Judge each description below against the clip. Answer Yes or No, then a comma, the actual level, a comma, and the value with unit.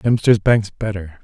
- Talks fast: No, average, 145 wpm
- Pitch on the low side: Yes, low, 105 Hz